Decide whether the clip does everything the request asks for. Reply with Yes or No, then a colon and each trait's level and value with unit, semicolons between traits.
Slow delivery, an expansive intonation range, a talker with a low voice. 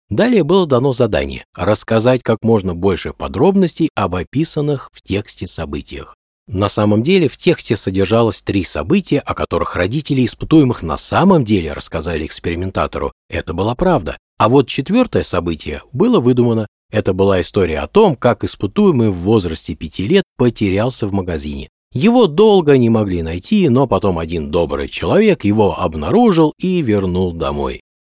No: average, 150 wpm; wide, 8.2 semitones; low, 110 Hz